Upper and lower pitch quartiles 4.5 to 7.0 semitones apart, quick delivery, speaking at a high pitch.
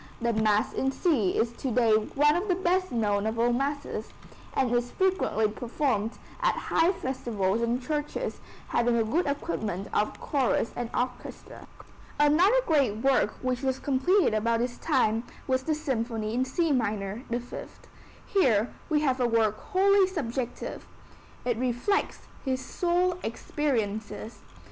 No: average, 4.9 semitones; average, 150 wpm; very high, 250 Hz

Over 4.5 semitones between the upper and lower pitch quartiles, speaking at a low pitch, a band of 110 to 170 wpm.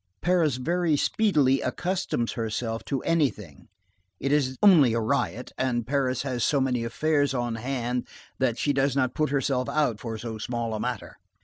No: average, 3.7 semitones; low, 130 Hz; average, 155 wpm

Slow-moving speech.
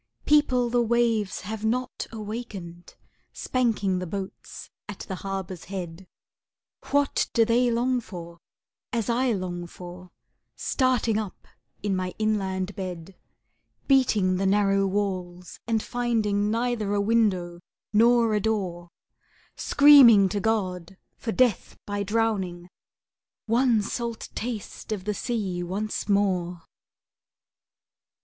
Yes: slow, 115 wpm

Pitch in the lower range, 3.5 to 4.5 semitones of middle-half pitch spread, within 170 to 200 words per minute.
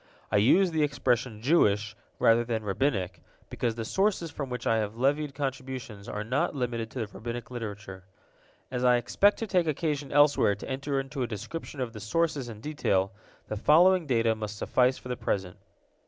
No: low, 125 Hz; average, 5.0 semitones; average, 185 wpm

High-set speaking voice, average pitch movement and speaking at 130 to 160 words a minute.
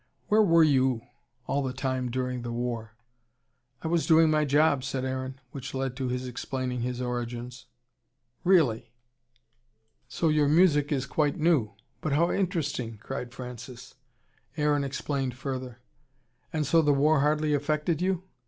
No: low, 135 Hz; average, 3.4 semitones; average, 145 wpm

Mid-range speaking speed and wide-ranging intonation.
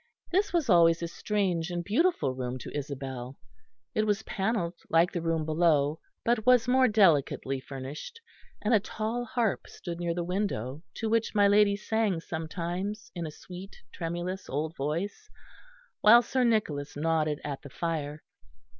Yes: average, 155 wpm; wide, 5.8 semitones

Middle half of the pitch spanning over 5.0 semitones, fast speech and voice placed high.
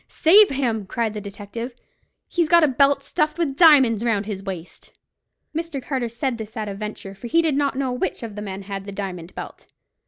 Yes: wide, 5.6 semitones; fast, 210 wpm; high, 235 Hz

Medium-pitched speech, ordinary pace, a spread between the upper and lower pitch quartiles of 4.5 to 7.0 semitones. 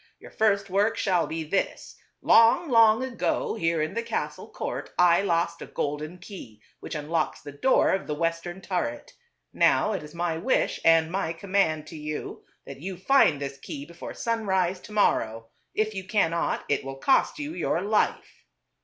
Yes: medium, 175 Hz; average, 175 wpm; average, 5.0 semitones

